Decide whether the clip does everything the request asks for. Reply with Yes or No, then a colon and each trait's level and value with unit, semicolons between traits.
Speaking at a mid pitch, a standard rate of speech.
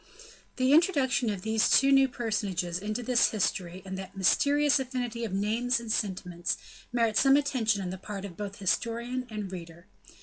No: high, 220 Hz; average, 170 wpm